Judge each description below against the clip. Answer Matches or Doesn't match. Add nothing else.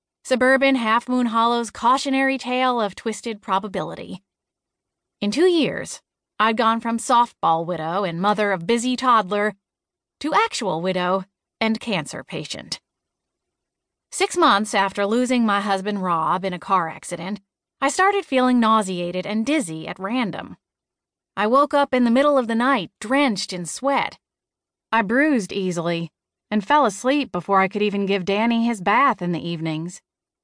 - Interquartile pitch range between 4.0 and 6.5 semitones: Matches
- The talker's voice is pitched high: Matches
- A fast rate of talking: Doesn't match